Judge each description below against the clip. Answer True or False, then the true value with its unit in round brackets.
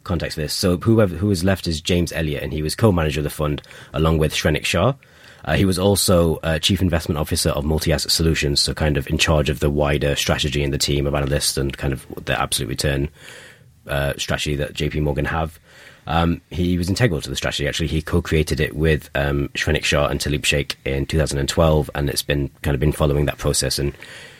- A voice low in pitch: True (75 Hz)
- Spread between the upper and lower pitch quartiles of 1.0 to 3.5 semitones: True (2.5 semitones)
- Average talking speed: False (220 wpm)